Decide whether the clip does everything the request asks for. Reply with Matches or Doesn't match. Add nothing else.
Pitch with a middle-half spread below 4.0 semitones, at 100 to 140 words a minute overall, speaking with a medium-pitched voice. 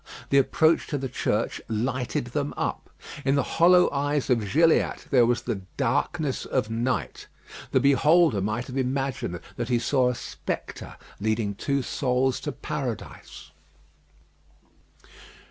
Doesn't match